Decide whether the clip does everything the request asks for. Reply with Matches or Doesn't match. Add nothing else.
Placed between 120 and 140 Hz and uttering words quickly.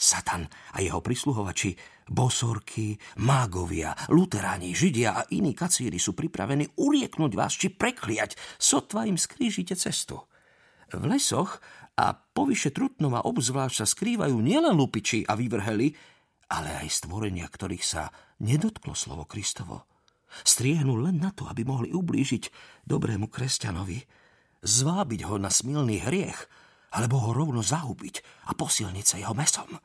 Doesn't match